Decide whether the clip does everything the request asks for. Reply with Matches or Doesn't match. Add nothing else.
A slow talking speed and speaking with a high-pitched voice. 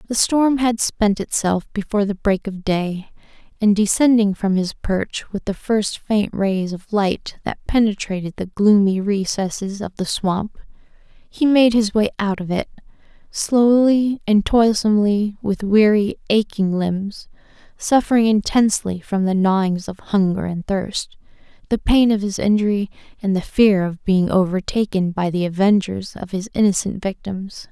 Doesn't match